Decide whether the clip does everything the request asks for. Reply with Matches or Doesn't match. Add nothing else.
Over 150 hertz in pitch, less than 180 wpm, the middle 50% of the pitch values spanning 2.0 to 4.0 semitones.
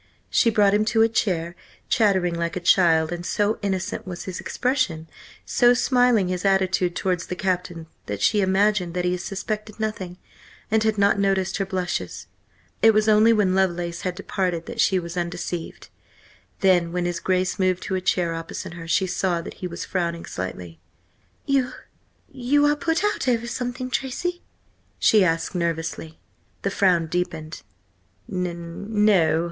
Matches